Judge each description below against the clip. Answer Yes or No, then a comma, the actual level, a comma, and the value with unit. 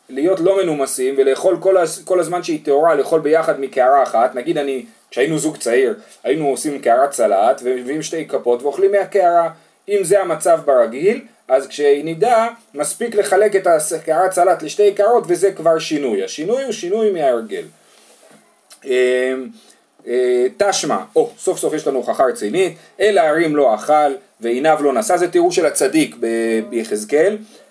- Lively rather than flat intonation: Yes, wide, 6.2 semitones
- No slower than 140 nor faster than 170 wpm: Yes, average, 145 wpm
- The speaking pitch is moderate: Yes, medium, 175 Hz